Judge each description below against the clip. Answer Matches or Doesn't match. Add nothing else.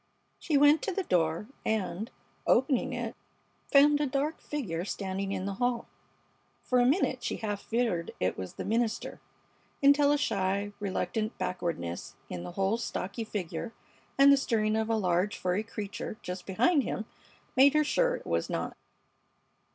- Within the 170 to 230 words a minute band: Doesn't match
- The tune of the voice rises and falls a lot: Matches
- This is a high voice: Matches